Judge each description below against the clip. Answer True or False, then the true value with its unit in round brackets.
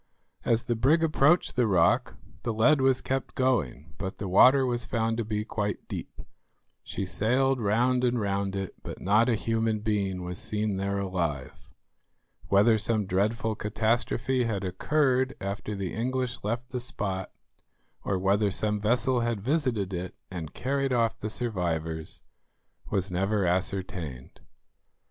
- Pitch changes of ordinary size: True (4.1 semitones)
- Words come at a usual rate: True (150 wpm)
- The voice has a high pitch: False (110 Hz)